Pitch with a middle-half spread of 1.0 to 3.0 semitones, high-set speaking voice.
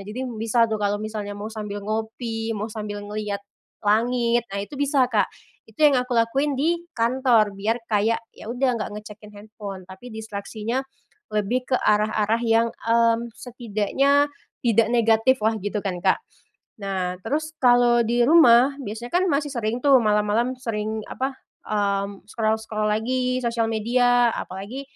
Yes: average, 2.7 semitones; high, 225 Hz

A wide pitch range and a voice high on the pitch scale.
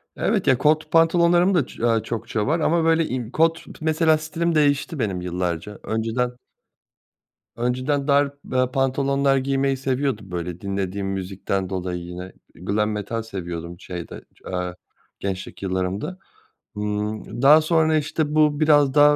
No: wide, 7.5 semitones; low, 125 Hz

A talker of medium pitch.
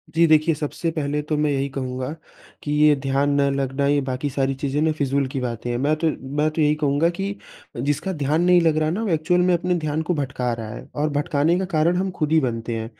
Yes: medium, 150 Hz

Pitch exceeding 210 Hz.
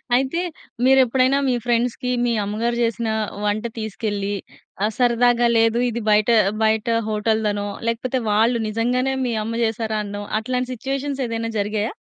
Yes: high, 230 Hz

